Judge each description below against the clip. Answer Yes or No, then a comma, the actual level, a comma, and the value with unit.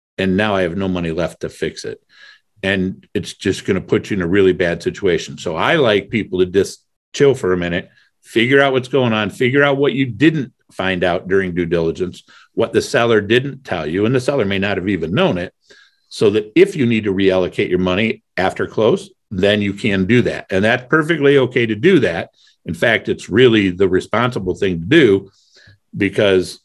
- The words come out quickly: Yes, fast, 215 wpm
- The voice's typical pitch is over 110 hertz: No, low, 105 Hz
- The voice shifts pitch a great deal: Yes, wide, 6.4 semitones